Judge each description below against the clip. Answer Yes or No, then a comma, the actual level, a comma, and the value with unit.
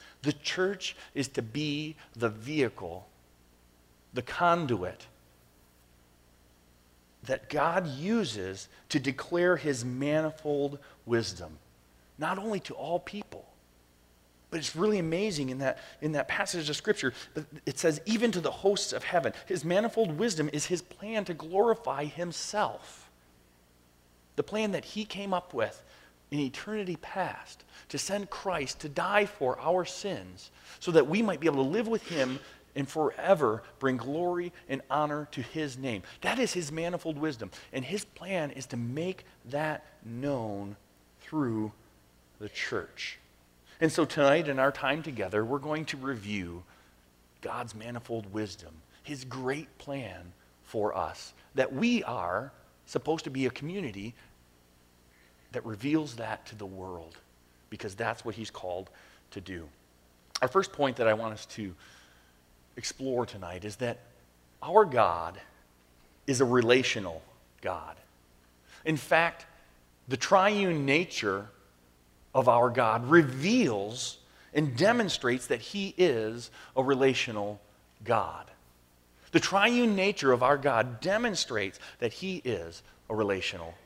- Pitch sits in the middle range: No, low, 130 Hz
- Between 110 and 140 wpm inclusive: Yes, slow, 135 wpm